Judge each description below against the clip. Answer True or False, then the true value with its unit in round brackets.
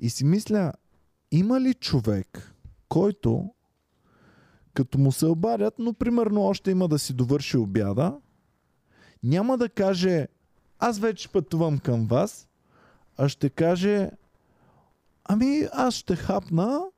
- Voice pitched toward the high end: False (170 Hz)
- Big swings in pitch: True (8.0 semitones)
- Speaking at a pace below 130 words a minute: True (120 wpm)